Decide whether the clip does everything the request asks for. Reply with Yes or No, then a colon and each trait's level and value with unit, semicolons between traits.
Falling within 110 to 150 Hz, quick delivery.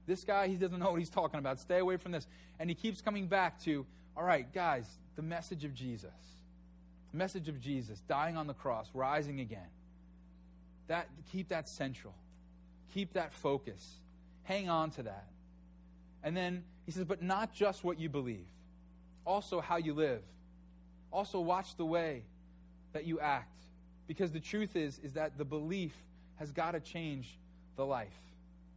No: medium, 140 Hz; average, 170 wpm